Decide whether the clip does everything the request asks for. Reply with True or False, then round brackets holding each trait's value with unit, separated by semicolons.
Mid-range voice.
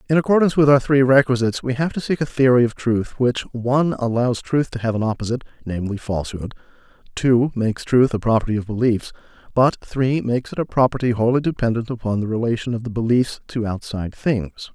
False (120 Hz)